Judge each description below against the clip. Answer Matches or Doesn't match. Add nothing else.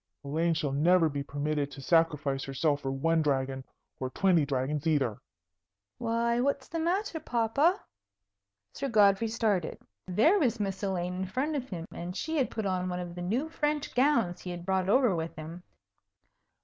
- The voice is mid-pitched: Matches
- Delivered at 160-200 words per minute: Matches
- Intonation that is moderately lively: Doesn't match